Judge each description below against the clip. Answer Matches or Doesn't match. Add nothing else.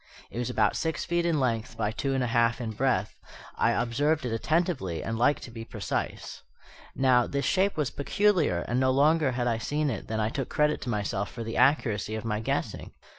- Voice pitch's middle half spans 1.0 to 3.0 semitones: Doesn't match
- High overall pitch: Doesn't match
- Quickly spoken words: Matches